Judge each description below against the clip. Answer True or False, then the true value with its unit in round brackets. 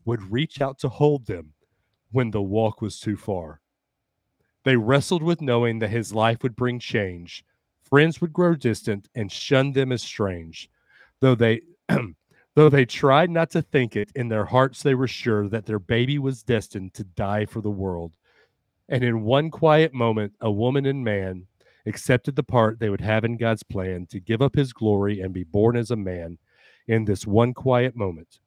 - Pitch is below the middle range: True (115 Hz)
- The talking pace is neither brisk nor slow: True (190 wpm)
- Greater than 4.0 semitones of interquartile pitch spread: True (4.4 semitones)